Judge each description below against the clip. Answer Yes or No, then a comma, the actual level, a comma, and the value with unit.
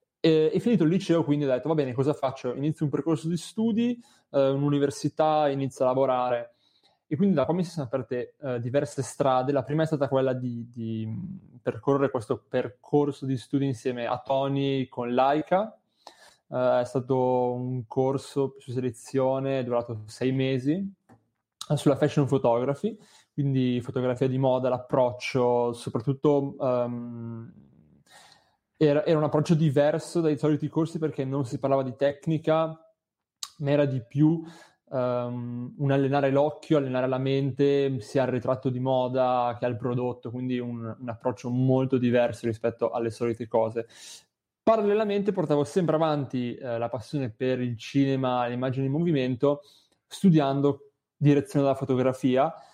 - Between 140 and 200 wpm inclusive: Yes, average, 150 wpm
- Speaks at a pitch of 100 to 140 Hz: Yes, low, 135 Hz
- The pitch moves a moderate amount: Yes, average, 3.0 semitones